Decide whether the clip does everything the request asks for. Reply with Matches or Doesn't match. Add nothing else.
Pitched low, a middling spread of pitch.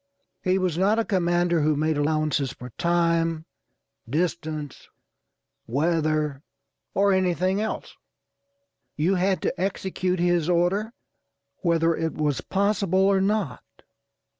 Doesn't match